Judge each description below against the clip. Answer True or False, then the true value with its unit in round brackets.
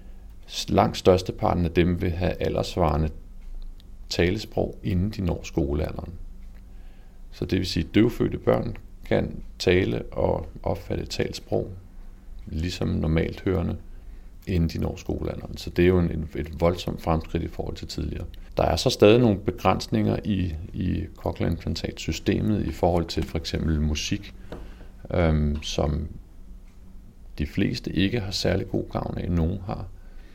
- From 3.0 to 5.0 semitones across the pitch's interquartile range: False (2.6 semitones)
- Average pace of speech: False (140 wpm)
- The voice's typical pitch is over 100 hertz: False (90 Hz)